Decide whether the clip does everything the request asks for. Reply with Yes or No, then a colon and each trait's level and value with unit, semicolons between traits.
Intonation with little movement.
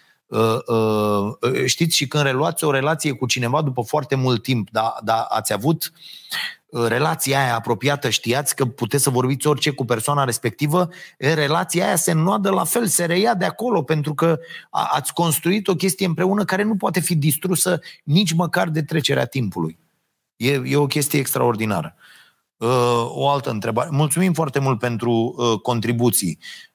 No: wide, 5.5 semitones